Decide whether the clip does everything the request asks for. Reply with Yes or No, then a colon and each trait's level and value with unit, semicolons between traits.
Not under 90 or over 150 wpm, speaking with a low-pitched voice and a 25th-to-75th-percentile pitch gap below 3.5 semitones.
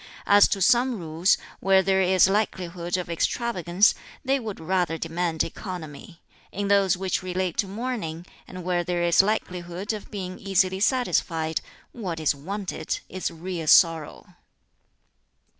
No: average, 140 wpm; medium, 185 Hz; average, 2.7 semitones